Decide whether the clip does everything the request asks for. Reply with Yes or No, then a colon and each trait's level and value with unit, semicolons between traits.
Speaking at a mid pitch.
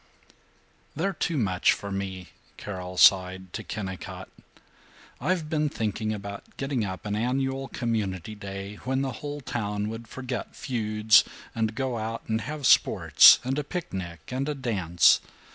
No: low, 110 Hz